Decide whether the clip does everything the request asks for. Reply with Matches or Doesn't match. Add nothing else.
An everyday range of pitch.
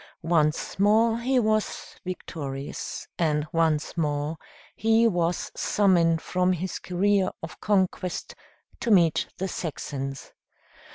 Matches